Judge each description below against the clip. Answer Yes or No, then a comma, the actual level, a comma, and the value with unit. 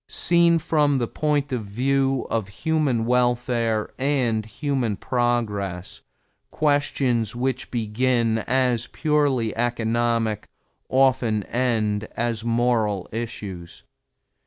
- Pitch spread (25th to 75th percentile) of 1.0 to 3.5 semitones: Yes, average, 3.1 semitones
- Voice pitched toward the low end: Yes, low, 120 Hz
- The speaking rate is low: Yes, slow, 95 wpm